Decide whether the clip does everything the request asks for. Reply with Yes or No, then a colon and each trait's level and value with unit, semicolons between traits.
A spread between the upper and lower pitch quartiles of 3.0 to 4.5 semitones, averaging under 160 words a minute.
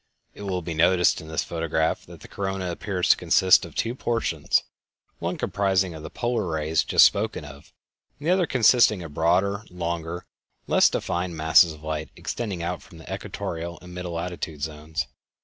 No: average, 3.3 semitones; average, 185 wpm